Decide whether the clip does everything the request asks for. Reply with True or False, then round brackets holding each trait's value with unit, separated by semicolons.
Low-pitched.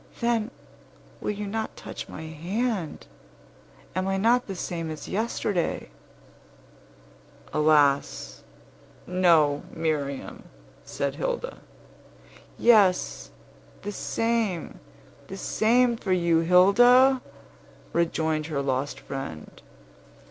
False (185 Hz)